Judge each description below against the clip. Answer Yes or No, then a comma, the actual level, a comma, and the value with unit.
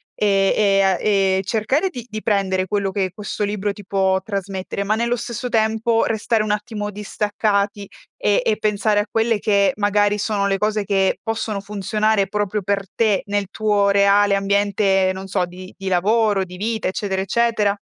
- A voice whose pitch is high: Yes, high, 205 Hz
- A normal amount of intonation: No, narrow, 1.7 semitones